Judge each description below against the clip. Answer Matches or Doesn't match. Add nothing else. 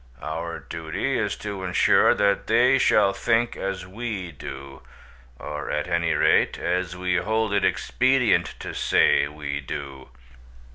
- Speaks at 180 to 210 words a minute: Doesn't match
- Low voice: Matches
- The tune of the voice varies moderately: Doesn't match